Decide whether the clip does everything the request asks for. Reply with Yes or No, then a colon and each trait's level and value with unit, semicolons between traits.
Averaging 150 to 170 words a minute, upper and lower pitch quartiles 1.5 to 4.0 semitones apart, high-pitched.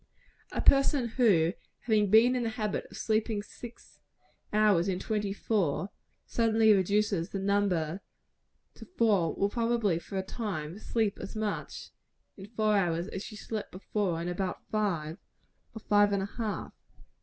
Yes: average, 155 wpm; narrow, 2.6 semitones; high, 205 Hz